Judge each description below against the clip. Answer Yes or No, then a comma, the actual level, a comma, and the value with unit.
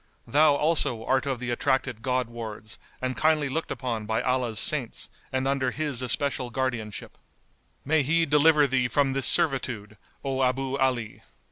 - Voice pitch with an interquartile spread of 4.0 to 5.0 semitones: No, average, 2.8 semitones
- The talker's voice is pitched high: No, low, 130 Hz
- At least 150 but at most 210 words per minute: Yes, average, 160 wpm